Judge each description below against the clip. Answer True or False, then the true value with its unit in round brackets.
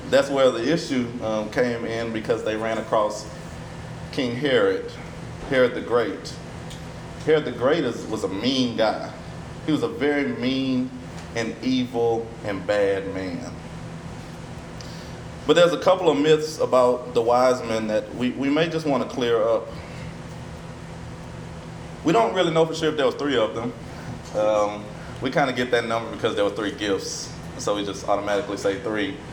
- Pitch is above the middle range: False (125 Hz)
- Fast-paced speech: False (170 wpm)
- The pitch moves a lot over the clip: True (5.8 semitones)